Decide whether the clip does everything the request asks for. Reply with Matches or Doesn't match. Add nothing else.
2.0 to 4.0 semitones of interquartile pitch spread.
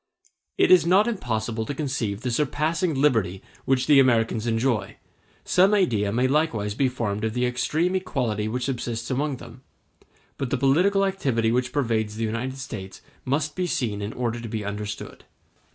Doesn't match